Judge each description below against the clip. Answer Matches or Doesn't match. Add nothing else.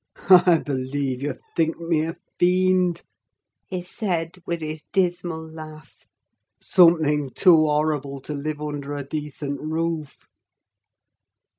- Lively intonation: Doesn't match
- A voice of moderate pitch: Matches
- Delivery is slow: Matches